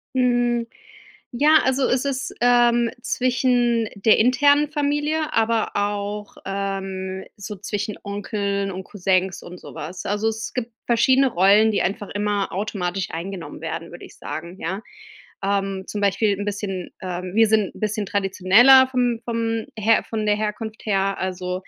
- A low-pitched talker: No, high, 210 Hz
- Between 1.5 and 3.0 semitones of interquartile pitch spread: No, average, 3.7 semitones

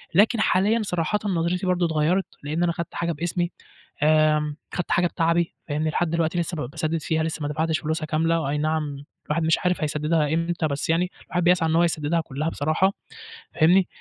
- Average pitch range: No, narrow, 2.1 semitones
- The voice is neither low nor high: Yes, medium, 165 Hz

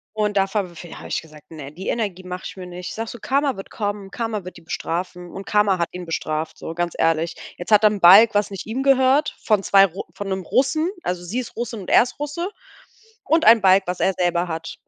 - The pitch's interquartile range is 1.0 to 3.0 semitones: No, average, 4.1 semitones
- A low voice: No, high, 195 Hz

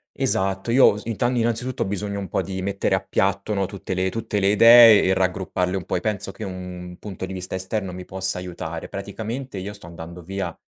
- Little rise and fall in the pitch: Yes, narrow, 2.3 semitones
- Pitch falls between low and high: No, very low, 95 Hz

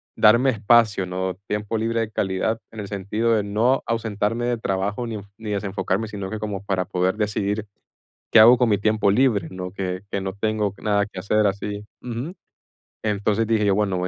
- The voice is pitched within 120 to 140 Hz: No, low, 105 Hz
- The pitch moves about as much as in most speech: No, narrow, 2.2 semitones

